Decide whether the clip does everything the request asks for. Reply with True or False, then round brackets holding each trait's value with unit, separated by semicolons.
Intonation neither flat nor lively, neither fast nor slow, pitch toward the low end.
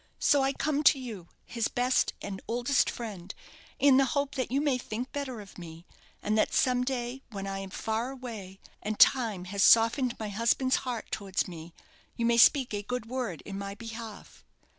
False (4.3 semitones; 190 wpm; 230 Hz)